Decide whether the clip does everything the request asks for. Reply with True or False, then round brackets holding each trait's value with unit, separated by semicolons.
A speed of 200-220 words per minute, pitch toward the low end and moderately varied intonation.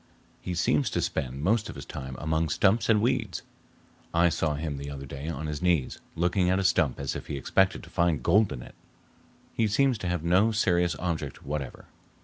True (205 wpm; 85 Hz; 5.0 semitones)